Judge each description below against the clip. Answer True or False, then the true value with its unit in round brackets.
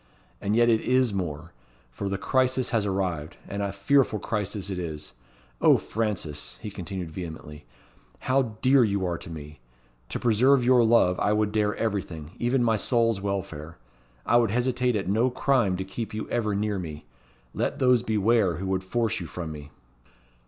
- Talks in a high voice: False (105 Hz)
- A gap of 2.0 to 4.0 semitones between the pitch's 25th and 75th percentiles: False (4.7 semitones)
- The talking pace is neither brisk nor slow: True (175 wpm)